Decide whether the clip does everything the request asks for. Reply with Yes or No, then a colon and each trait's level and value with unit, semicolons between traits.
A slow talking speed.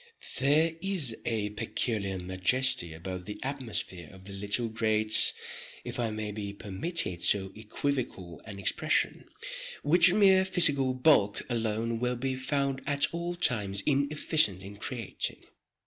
Yes: slow, 125 wpm